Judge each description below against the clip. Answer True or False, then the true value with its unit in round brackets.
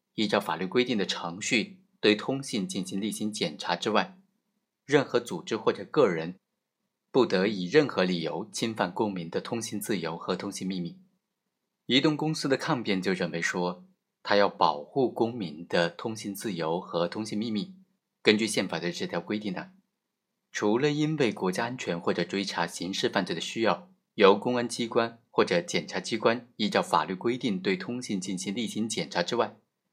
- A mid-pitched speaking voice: False (120 Hz)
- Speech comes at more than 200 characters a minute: True (265 characters per minute)